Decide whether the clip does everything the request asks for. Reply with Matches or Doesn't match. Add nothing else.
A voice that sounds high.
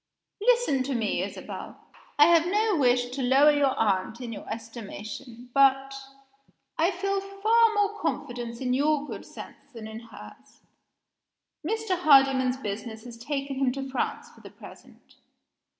Matches